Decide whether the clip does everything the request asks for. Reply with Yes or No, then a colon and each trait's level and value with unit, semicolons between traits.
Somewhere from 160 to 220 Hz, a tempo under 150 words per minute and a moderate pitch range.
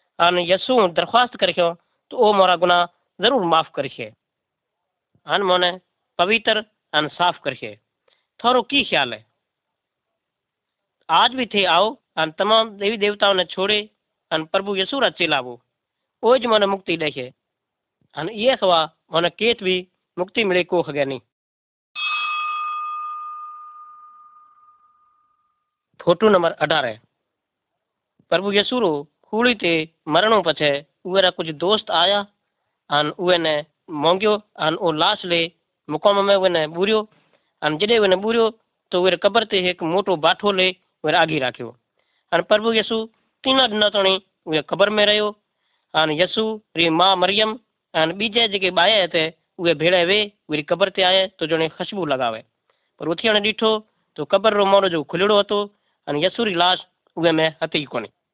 Yes: high, 190 Hz; average, 140 wpm; average, 4.6 semitones